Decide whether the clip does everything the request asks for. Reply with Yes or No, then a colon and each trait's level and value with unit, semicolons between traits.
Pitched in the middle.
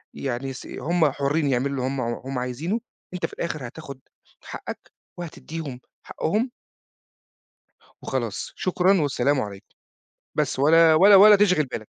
Yes: medium, 145 Hz